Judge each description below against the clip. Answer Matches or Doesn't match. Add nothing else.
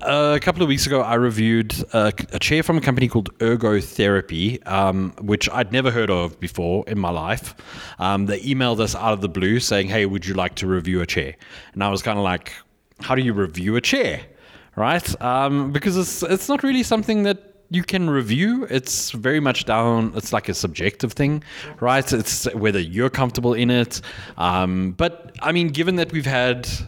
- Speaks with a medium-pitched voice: Doesn't match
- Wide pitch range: Matches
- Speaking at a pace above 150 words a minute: Matches